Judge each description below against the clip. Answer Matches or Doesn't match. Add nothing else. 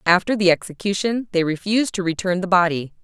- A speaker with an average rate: Matches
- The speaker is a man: Doesn't match